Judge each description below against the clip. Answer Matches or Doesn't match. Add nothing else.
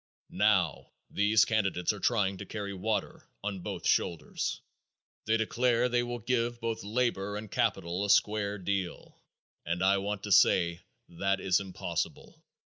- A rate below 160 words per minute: Matches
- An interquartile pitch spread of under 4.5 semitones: Matches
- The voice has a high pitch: Doesn't match